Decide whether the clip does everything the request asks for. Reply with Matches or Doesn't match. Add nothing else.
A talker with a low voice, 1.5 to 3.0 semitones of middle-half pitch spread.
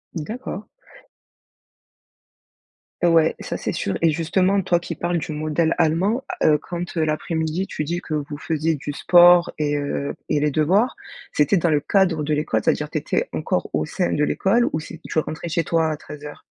Doesn't match